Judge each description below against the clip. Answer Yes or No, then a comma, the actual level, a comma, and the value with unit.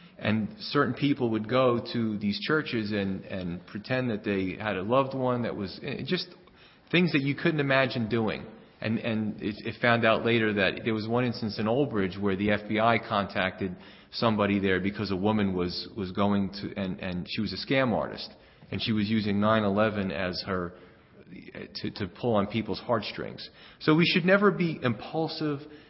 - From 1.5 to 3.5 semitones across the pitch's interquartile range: No, average, 4.3 semitones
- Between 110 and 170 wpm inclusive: No, average, 185 wpm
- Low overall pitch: Yes, low, 110 Hz